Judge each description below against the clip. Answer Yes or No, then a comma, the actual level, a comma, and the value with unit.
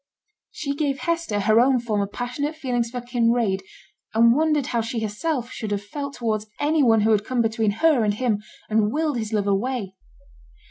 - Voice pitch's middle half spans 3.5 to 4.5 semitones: Yes, average, 4.2 semitones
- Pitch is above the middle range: Yes, high, 235 Hz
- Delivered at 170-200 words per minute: Yes, average, 185 wpm